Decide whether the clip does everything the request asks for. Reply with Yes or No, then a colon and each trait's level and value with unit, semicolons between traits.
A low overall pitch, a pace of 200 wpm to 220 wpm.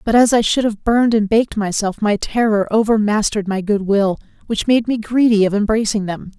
No: high, 215 Hz; fast, 205 wpm